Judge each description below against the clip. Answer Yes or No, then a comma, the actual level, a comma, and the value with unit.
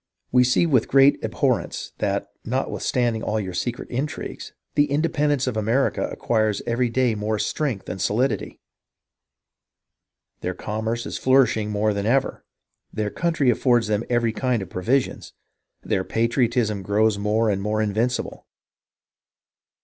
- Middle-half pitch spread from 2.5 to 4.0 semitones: Yes, average, 3.3 semitones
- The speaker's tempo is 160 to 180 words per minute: No, slow, 135 wpm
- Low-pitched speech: Yes, low, 115 Hz